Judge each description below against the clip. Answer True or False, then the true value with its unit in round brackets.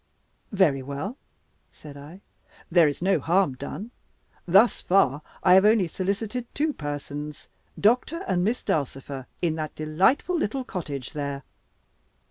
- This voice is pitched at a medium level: True (175 Hz)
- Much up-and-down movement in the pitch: True (6.1 semitones)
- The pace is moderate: False (130 wpm)